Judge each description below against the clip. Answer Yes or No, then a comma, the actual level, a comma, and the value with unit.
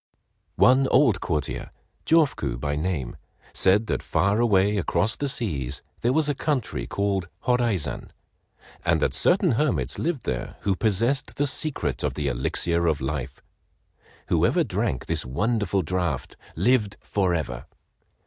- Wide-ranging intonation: Yes, wide, 8.5 semitones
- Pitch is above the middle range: No, very low, 95 Hz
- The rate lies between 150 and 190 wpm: No, average, 140 wpm